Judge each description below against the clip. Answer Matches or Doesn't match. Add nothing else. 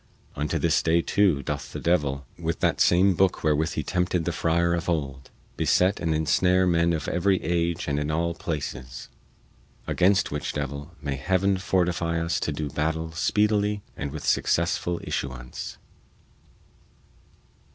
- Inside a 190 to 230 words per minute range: Doesn't match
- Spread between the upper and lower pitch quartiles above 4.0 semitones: Doesn't match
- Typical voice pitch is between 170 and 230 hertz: Doesn't match